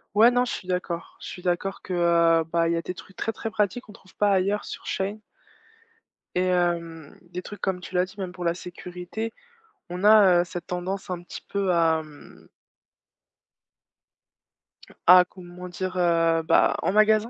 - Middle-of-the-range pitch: Yes, medium, 180 Hz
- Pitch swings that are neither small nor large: No, narrow, 2.3 semitones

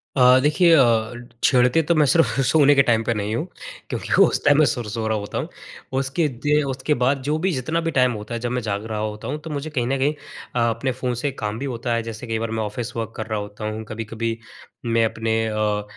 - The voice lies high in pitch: No, low, 120 Hz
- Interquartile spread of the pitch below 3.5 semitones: No, average, 3.8 semitones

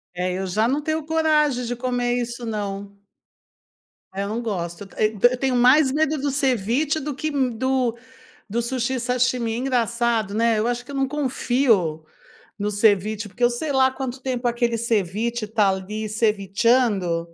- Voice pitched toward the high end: Yes, high, 235 Hz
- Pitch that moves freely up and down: No, average, 3.7 semitones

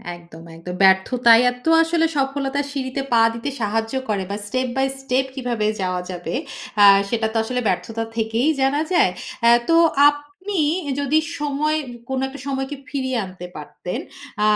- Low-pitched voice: No, very high, 250 Hz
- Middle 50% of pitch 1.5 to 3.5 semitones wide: No, average, 4.4 semitones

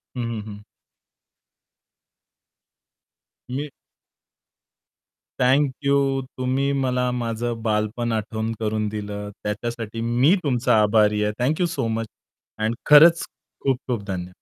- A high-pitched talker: No, low, 115 Hz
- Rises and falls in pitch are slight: No, average, 3.6 semitones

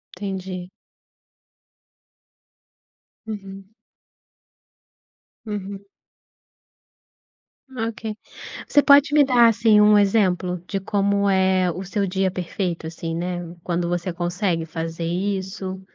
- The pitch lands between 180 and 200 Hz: Yes, high, 190 Hz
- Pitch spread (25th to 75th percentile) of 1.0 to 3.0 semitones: Yes, narrow, 2.6 semitones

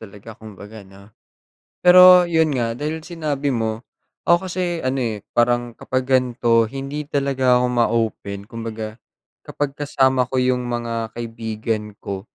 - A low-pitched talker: Yes, low, 120 Hz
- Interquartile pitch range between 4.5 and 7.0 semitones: No, average, 3.8 semitones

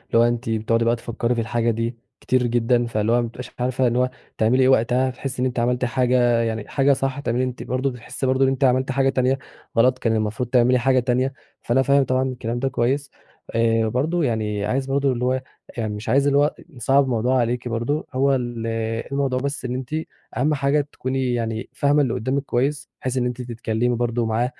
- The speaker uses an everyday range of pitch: No, narrow, 2.1 semitones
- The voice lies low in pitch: Yes, low, 125 Hz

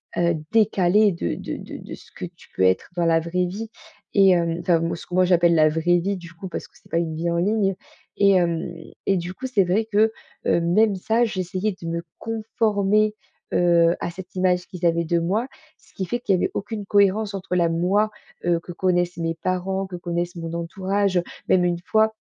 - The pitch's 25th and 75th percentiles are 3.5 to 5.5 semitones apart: No, average, 2.8 semitones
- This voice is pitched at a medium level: Yes, medium, 180 Hz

